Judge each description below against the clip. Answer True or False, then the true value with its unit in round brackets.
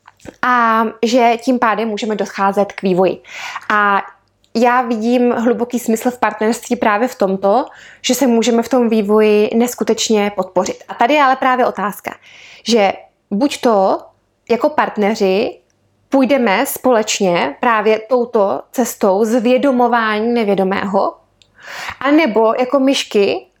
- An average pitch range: True (3.1 semitones)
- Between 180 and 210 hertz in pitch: False (230 Hz)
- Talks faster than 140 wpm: False (120 wpm)